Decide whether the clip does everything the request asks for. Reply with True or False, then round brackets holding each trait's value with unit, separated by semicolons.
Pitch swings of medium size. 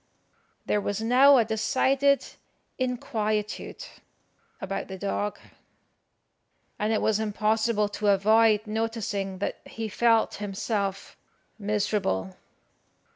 False (2.0 semitones)